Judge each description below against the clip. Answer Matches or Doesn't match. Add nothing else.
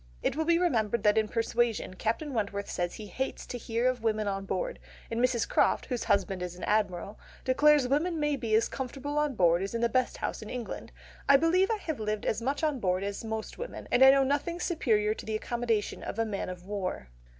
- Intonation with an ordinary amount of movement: Matches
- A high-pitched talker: Matches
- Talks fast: Matches